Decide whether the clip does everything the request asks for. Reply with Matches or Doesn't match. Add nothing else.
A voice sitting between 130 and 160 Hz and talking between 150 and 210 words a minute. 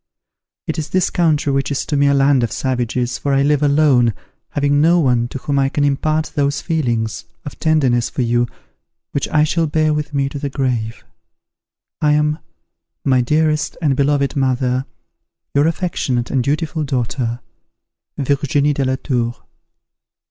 Matches